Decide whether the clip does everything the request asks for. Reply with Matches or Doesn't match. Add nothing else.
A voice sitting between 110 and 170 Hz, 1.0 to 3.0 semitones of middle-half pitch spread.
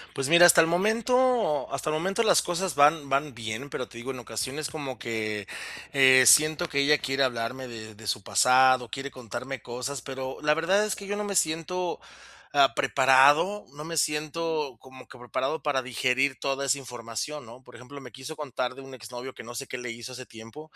Doesn't match